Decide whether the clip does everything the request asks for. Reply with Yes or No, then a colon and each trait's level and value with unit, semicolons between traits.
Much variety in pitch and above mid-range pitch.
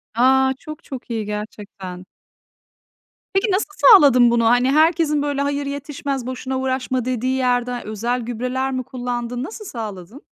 No: average, 2.9 semitones; very high, 255 Hz